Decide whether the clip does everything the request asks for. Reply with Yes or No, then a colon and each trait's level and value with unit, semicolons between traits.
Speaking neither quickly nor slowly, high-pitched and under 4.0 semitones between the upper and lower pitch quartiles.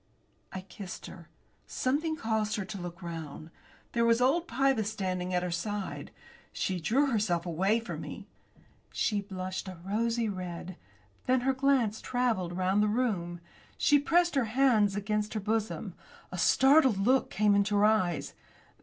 No: average, 155 wpm; high, 210 Hz; average, 4.8 semitones